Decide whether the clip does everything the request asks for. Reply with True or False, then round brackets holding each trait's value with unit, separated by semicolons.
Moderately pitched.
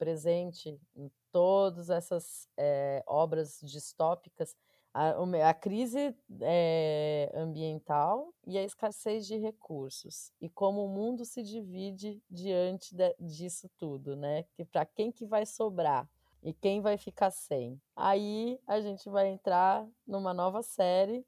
True (180 Hz)